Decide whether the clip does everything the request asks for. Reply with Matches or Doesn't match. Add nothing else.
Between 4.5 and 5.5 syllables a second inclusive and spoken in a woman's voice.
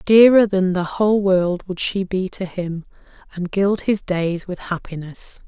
Doesn't match